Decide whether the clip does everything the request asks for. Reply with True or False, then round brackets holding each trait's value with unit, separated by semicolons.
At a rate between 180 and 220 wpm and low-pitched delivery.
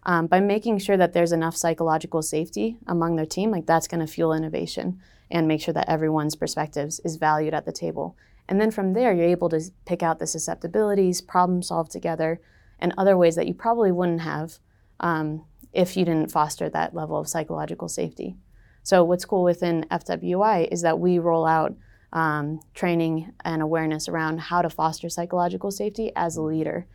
False (185 wpm; 165 Hz)